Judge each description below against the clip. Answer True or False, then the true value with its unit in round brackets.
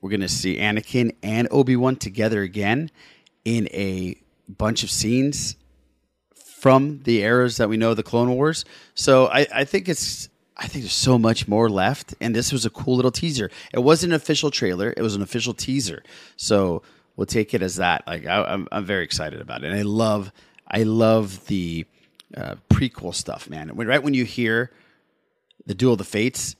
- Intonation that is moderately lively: True (4.0 semitones)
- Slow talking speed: False (190 wpm)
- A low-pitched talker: True (115 Hz)